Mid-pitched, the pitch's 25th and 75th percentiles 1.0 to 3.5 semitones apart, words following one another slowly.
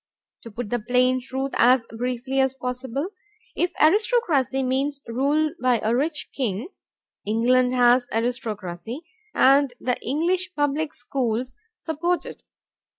No: very high, 255 Hz; average, 3.0 semitones; slow, 125 wpm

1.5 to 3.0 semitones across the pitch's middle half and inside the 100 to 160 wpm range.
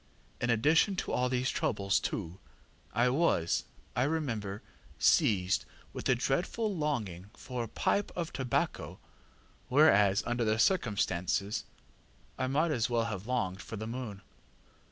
No: average, 5.2 semitones; slow, 135 wpm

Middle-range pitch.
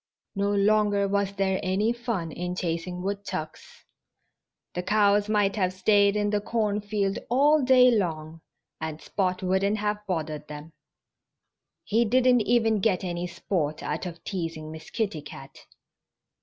No: high, 200 Hz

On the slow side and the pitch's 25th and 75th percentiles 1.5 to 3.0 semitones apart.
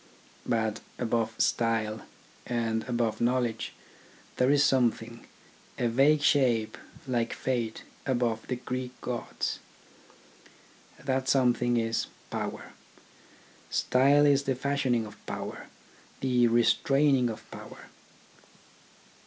Yes: slow, 100 wpm; narrow, 2.5 semitones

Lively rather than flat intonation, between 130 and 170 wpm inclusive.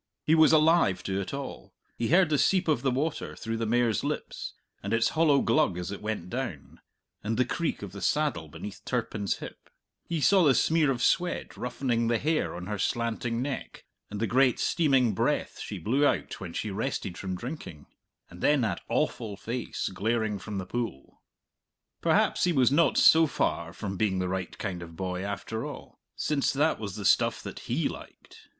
No: wide, 6.4 semitones; average, 195 wpm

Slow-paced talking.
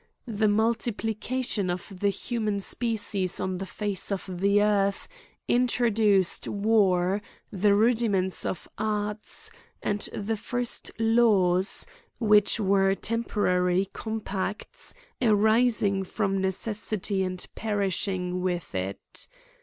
Yes: slow, 105 wpm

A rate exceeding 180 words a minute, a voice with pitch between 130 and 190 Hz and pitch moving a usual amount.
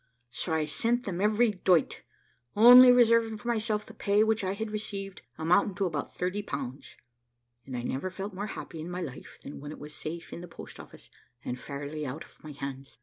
No: fast, 205 wpm; medium, 185 Hz; wide, 5.9 semitones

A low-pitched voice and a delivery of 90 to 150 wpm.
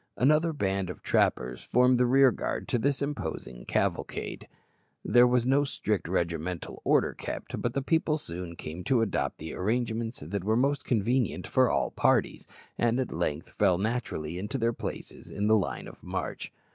No: low, 115 Hz; average, 170 wpm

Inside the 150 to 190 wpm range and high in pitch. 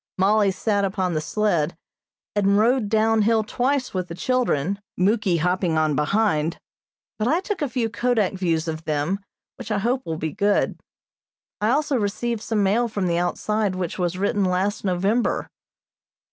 Yes: average, 165 wpm; high, 200 Hz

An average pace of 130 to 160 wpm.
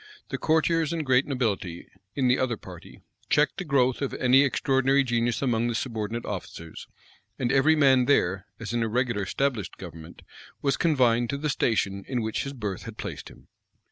No: average, 180 wpm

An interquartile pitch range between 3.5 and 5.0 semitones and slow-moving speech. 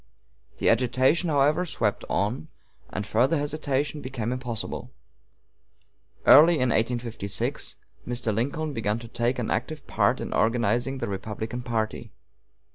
Yes: average, 3.8 semitones; slow, 120 wpm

